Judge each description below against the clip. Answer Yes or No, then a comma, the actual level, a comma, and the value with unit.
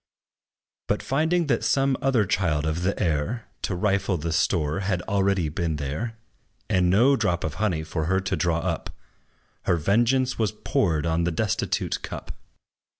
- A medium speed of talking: Yes, average, 160 wpm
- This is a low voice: Yes, very low, 95 Hz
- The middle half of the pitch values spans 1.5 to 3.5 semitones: No, average, 5.2 semitones